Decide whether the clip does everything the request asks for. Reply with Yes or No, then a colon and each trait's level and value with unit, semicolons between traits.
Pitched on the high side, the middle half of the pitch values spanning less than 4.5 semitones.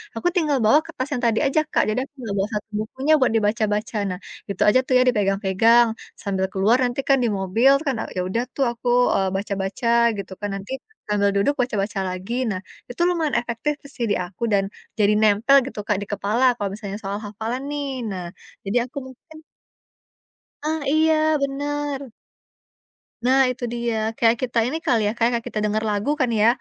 No: high, 230 Hz; average, 4.8 semitones